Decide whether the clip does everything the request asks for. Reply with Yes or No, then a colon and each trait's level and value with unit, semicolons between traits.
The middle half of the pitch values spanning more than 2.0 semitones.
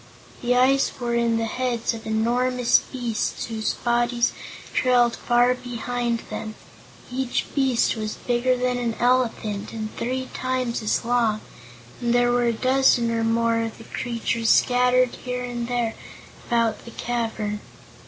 No: narrow, 1.5 semitones